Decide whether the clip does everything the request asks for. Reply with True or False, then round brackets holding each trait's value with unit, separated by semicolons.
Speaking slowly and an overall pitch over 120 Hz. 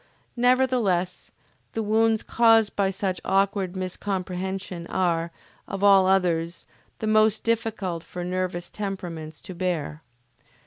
True (110 wpm; 190 Hz)